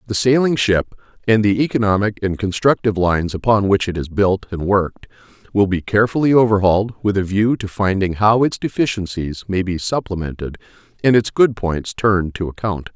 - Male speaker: Yes, male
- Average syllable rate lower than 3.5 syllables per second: No, 5.5 syllables/s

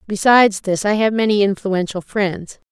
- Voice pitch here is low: No, high, 200 Hz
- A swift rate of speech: No, average, 155 wpm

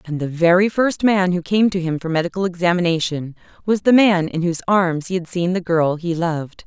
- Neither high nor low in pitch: Yes, medium, 175 Hz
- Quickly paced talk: Yes, fast, 225 wpm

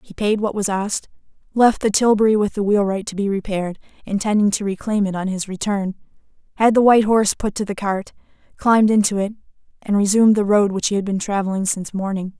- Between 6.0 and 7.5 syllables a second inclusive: Yes, 6.3 syllables/s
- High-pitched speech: Yes, high, 205 Hz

